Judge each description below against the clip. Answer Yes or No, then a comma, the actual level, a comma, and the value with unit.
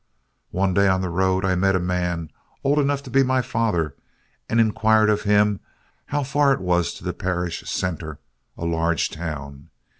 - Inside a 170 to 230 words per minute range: Yes, average, 180 wpm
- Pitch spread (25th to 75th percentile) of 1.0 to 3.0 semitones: No, average, 4.5 semitones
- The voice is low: Yes, very low, 95 Hz